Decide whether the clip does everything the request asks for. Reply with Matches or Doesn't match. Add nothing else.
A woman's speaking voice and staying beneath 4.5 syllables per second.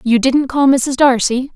Matches